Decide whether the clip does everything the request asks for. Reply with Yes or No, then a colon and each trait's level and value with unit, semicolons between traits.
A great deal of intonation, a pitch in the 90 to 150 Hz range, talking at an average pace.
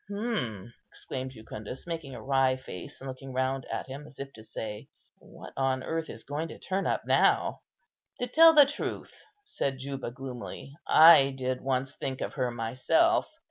No: average, 3.9 semitones; low, 135 Hz; average, 175 wpm